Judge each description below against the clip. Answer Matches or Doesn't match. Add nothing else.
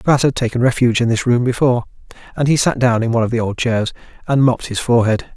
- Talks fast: Matches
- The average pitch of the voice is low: Matches